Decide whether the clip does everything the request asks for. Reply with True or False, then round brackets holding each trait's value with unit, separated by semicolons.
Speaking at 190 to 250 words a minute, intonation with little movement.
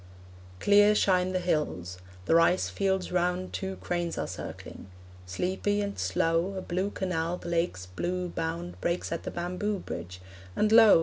False (160 wpm; 2.3 semitones)